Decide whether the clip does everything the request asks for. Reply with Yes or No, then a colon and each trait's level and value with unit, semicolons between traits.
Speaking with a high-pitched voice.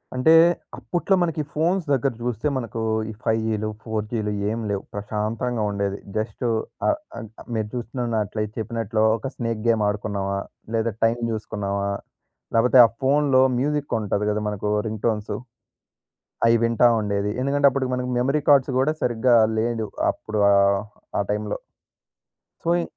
No: low, 115 Hz